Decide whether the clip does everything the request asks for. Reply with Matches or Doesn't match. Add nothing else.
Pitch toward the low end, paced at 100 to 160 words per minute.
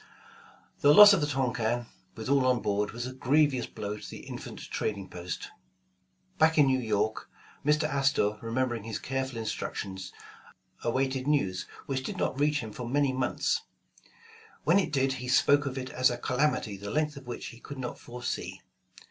Doesn't match